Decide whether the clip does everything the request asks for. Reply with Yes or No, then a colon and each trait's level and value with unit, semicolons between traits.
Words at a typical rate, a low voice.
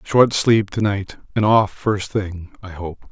Yes: average, 195 wpm; low, 100 Hz